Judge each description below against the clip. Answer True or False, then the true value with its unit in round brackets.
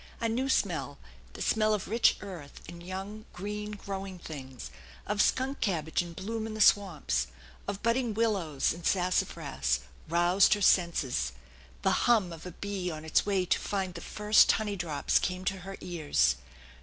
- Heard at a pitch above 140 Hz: True (190 Hz)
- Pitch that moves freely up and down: False (3.8 semitones)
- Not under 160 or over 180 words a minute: True (170 wpm)